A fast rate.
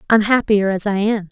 Yes: fast, 230 wpm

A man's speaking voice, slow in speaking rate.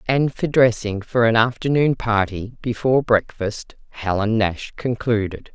No: female; slow, 130 wpm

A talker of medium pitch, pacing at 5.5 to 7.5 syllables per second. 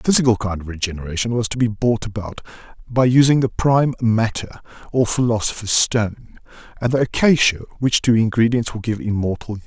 No: low, 115 Hz; 6.0 syllables/s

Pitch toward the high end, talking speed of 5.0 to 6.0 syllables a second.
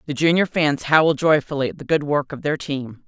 No: medium, 145 Hz; 5.5 syllables/s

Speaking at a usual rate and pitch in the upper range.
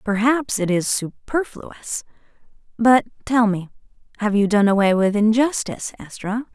No: slow, 110 wpm; high, 220 Hz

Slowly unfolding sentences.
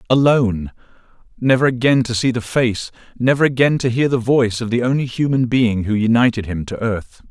No: average, 180 wpm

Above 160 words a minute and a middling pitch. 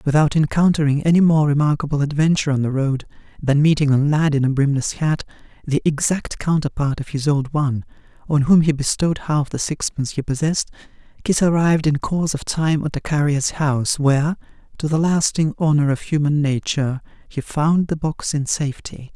Yes: average, 180 wpm; medium, 150 Hz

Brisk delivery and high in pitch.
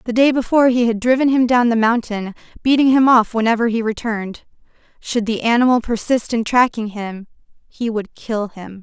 No: average, 185 wpm; high, 230 Hz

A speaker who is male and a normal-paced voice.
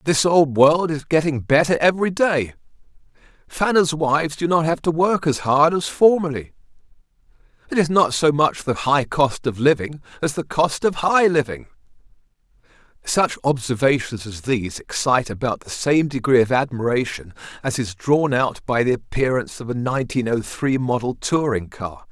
Yes: male; average, 165 wpm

